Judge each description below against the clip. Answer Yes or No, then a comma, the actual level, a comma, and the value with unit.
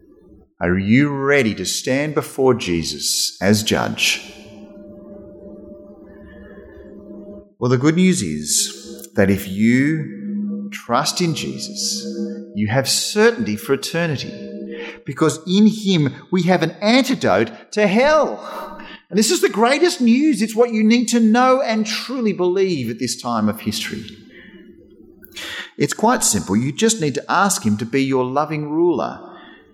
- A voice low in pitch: No, medium, 150 Hz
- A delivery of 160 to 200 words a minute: No, slow, 135 wpm